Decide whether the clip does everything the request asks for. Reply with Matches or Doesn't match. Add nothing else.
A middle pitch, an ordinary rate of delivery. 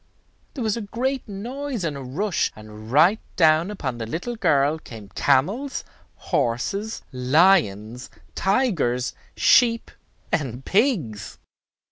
Doesn't match